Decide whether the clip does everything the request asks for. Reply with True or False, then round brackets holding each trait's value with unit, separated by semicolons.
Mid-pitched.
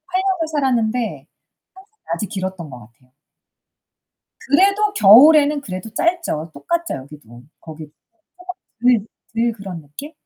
False (225 Hz)